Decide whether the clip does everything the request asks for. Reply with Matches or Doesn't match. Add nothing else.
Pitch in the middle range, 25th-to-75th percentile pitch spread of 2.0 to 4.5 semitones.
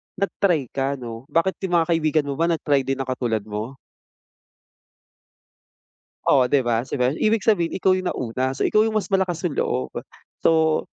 Doesn't match